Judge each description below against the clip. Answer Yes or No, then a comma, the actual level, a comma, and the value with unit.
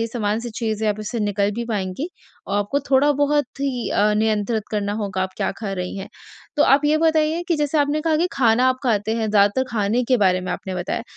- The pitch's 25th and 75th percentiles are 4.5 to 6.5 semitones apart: Yes, wide, 5.5 semitones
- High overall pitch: Yes, high, 225 Hz